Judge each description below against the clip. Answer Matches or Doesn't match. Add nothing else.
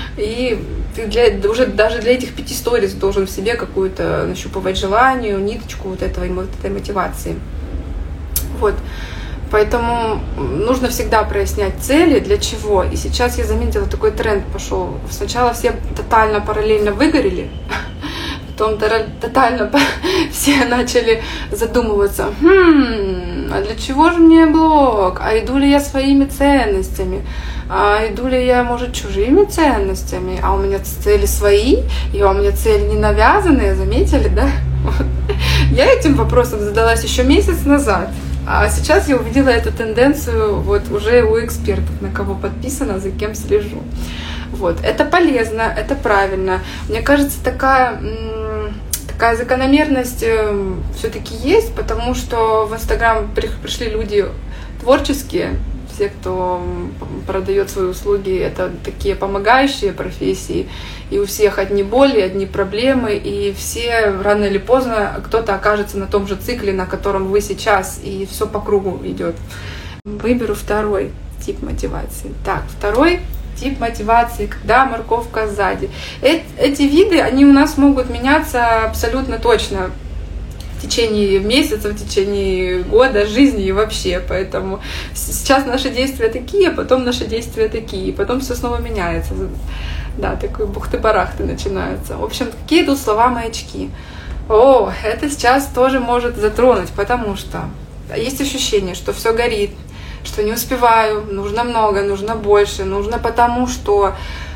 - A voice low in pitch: Doesn't match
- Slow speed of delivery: Doesn't match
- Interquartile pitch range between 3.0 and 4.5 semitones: Doesn't match